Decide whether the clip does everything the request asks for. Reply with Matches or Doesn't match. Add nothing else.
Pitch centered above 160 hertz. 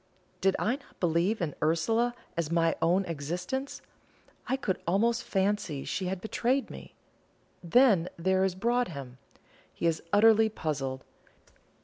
Matches